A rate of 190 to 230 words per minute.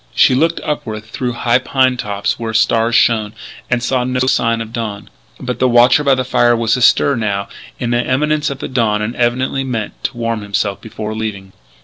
Yes: average, 200 wpm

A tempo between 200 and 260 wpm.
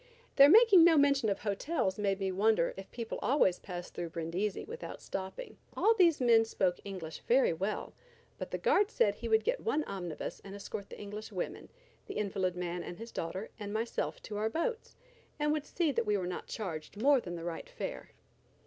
Yes: fast, 205 wpm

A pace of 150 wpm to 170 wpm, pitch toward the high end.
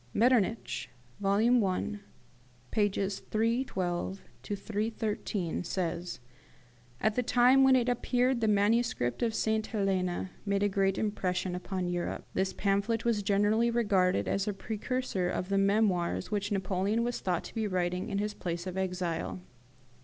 No: average, 140 wpm; high, 200 Hz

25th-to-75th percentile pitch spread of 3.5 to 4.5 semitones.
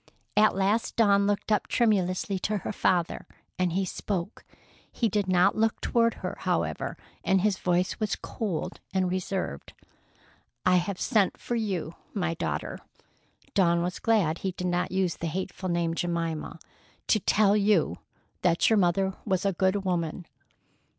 No: average, 2.7 semitones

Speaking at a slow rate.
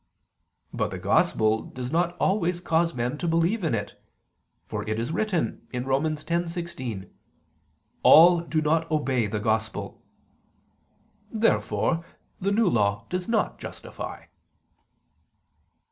Yes: slow, 115 wpm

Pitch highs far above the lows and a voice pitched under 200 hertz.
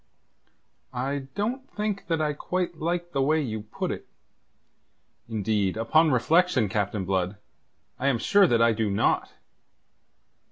Yes: wide, 8.1 semitones; low, 135 Hz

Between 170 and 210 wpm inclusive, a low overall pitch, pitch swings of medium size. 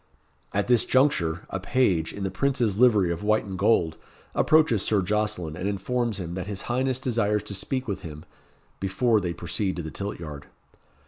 Yes: average, 185 wpm; low, 100 Hz; average, 4.8 semitones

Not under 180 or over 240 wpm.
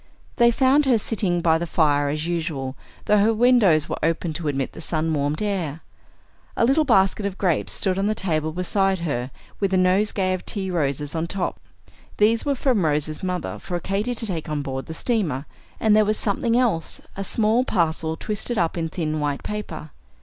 Yes: average, 195 wpm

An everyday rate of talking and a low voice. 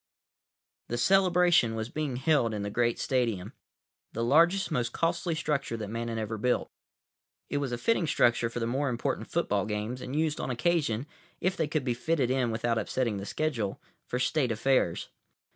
Yes: average, 185 wpm; low, 125 Hz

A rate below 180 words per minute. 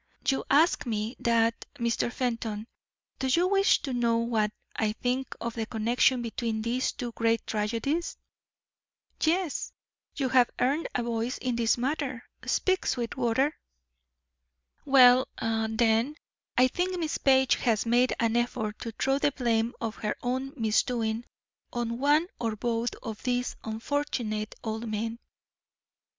Yes: slow, 135 wpm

